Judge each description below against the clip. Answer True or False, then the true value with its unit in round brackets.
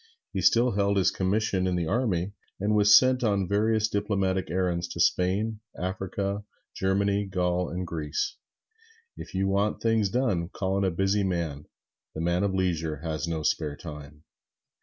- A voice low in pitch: True (95 Hz)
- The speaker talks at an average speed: True (160 wpm)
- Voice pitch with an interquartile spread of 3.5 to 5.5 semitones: False (2.8 semitones)